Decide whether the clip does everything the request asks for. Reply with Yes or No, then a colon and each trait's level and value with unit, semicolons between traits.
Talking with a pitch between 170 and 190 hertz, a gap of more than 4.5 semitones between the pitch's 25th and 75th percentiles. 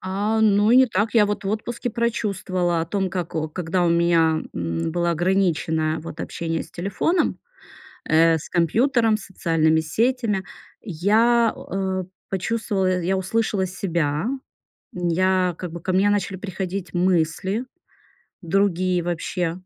No: medium, 185 Hz; average, 3.4 semitones